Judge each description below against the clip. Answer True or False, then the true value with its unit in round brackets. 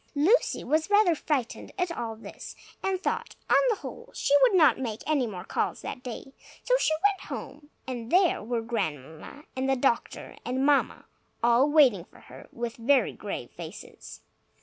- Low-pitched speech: False (270 Hz)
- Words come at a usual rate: True (170 wpm)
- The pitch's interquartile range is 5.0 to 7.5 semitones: True (5.3 semitones)